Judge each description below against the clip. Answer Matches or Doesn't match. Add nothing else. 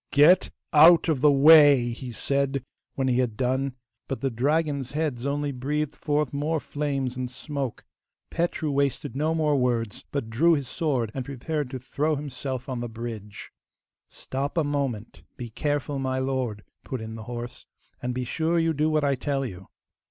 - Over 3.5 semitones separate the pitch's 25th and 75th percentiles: Doesn't match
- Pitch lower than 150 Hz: Matches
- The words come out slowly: Doesn't match